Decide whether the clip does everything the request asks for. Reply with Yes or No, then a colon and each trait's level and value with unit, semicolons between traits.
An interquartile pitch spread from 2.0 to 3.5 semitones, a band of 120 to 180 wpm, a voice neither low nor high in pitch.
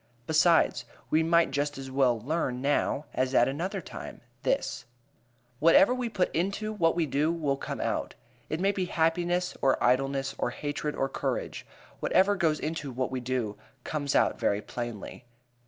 No: average, 4.2 semitones; average, 165 wpm; medium, 150 Hz